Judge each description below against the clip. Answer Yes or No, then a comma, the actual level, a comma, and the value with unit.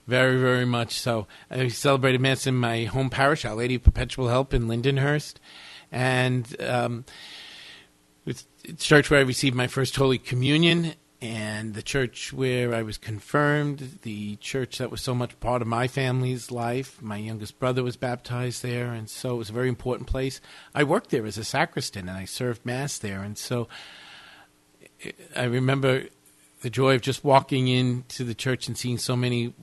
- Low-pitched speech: Yes, low, 125 Hz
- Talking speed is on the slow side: No, average, 180 wpm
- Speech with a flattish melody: Yes, narrow, 2.3 semitones